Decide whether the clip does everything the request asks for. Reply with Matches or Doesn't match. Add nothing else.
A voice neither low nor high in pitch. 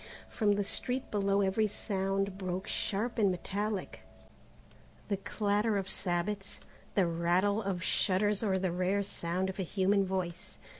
Doesn't match